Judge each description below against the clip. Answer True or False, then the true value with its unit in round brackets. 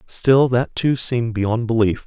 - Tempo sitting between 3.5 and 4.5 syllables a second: True (4.2 syllables/s)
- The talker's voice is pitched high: False (120 Hz)